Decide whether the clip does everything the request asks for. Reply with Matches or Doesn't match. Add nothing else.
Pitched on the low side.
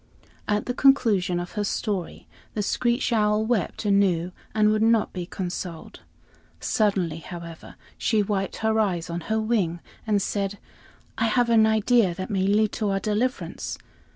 Doesn't match